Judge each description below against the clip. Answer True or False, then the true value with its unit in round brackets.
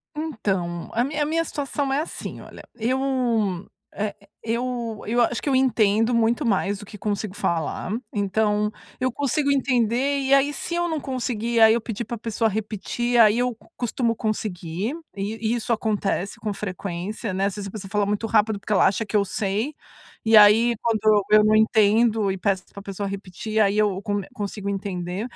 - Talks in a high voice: True (215 Hz)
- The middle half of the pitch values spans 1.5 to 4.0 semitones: True (3.0 semitones)